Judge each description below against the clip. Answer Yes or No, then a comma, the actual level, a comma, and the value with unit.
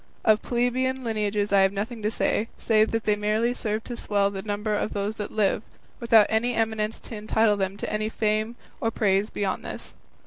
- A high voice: Yes, high, 215 Hz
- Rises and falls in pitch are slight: Yes, narrow, 1.5 semitones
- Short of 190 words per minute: No, average, 200 wpm